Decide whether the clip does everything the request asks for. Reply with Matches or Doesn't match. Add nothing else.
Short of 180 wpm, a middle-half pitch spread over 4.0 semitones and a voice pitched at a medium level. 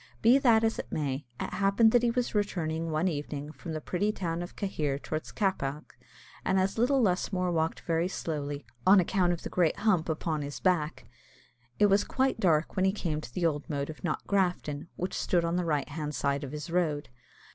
Doesn't match